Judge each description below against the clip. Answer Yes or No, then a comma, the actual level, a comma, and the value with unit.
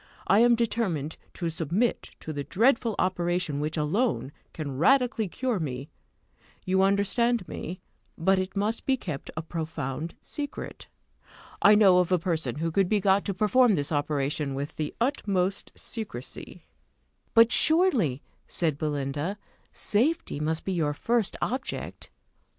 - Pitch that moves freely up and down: Yes, wide, 6.5 semitones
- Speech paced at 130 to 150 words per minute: Yes, average, 140 wpm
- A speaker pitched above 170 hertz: Yes, medium, 185 Hz